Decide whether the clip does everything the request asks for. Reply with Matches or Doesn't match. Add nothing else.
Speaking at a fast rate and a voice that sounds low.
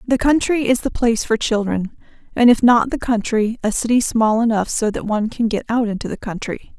Doesn't match